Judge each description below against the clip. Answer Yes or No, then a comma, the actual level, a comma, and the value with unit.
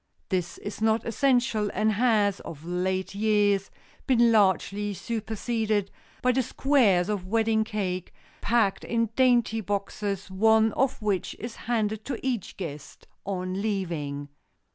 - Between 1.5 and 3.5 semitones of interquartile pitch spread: Yes, average, 3.1 semitones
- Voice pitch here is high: Yes, high, 210 Hz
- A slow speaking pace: Yes, slow, 130 wpm